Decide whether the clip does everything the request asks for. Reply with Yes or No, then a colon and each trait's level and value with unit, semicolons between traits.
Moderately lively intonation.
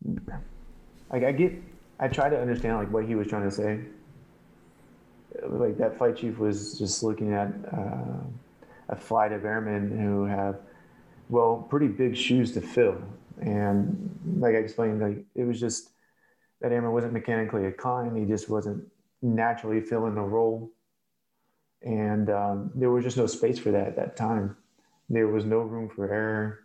No: narrow, 2.2 semitones